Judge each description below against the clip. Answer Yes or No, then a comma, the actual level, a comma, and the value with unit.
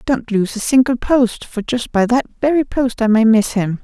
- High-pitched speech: Yes, high, 235 Hz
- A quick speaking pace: Yes, fast, 235 wpm